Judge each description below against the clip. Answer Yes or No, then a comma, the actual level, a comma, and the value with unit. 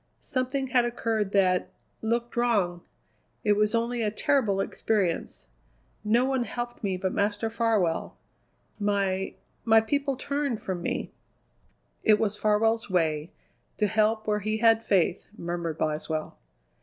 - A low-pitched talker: No, high, 215 Hz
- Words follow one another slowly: Yes, slow, 130 wpm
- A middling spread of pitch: Yes, average, 3.4 semitones